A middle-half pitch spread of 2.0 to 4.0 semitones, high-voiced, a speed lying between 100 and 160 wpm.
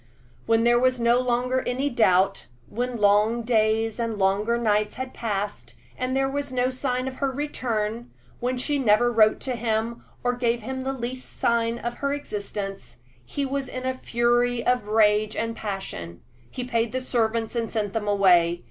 No: average, 2.9 semitones; high, 235 Hz; average, 175 wpm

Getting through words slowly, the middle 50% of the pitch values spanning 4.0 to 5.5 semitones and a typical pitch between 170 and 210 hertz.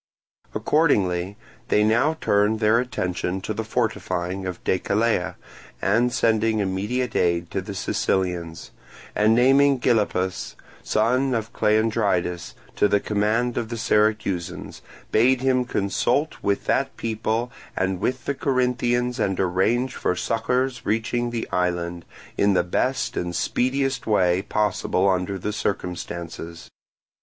No: slow, 125 wpm; average, 4.6 semitones; low, 105 Hz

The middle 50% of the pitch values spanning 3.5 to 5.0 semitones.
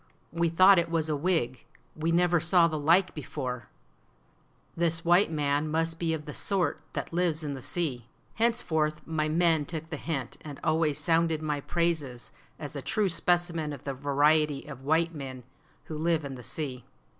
No: average, 2.7 semitones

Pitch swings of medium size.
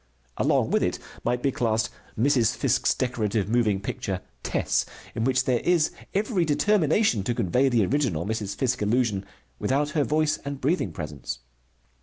No: wide, 5.7 semitones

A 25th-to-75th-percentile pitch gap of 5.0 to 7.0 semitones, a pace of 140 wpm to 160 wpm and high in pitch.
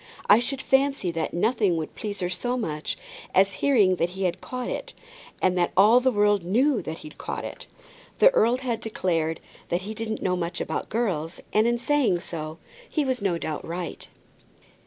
No: wide, 5.5 semitones; average, 190 wpm; high, 200 Hz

